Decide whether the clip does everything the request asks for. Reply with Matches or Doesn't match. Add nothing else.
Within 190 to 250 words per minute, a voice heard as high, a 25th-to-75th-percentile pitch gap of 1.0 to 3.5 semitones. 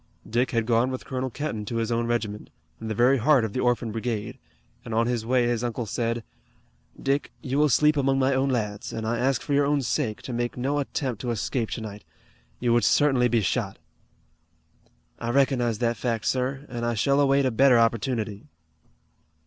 Doesn't match